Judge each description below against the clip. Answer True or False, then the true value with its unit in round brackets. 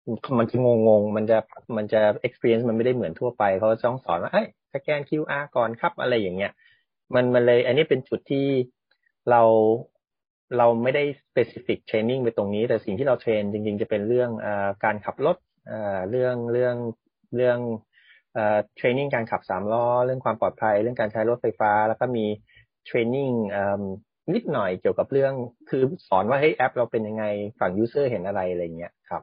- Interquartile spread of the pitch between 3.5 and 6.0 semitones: False (2.7 semitones)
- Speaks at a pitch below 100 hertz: False (115 Hz)